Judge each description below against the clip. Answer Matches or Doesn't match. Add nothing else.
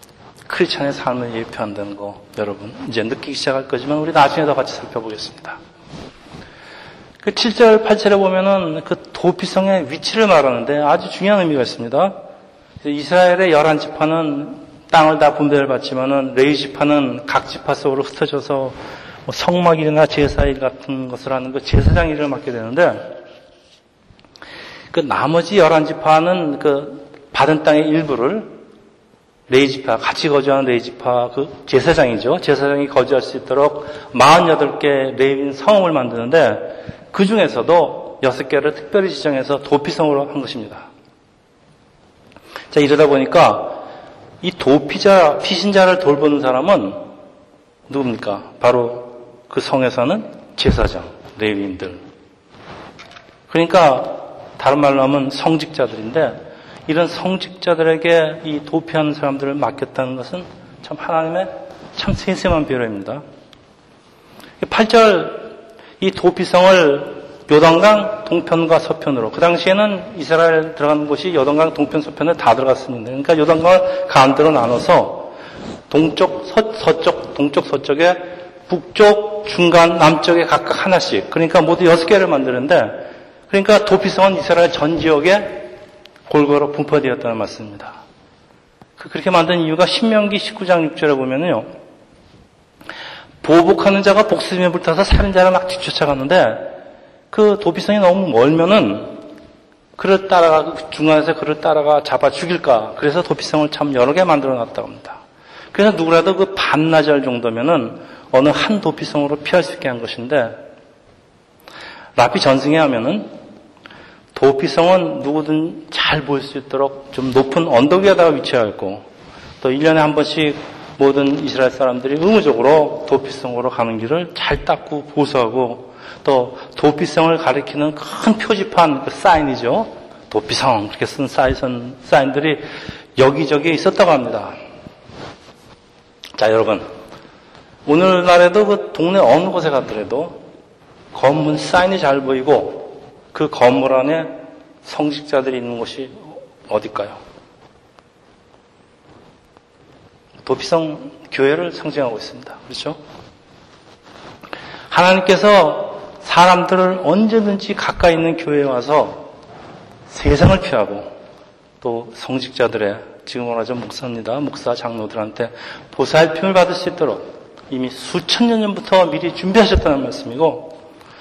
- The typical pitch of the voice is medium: Matches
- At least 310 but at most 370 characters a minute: Doesn't match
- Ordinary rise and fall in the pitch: Matches